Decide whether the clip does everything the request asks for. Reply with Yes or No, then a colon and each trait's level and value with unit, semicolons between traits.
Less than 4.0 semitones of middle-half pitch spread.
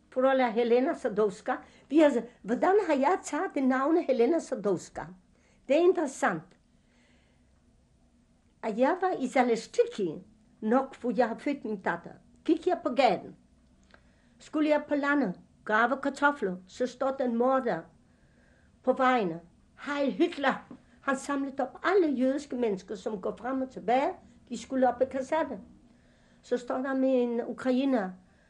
Yes: average, 3.3 semitones